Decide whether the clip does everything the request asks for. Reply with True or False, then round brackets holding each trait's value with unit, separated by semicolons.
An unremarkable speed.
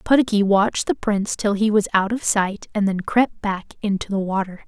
False (220 wpm)